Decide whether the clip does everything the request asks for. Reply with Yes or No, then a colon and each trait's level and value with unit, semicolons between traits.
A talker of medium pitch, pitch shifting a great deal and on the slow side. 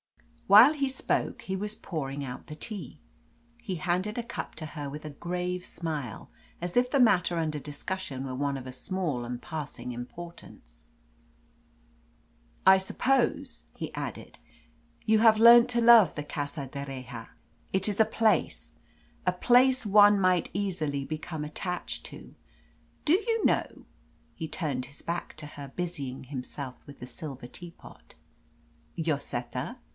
No: medium, 170 Hz; wide, 6.5 semitones; average, 145 wpm